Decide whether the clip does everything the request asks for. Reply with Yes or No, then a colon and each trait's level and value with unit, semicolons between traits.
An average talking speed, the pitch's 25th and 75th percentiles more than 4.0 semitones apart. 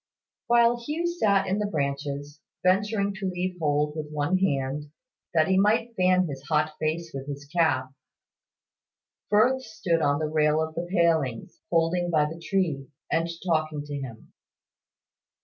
Yes: average, 150 wpm; average, 4.5 semitones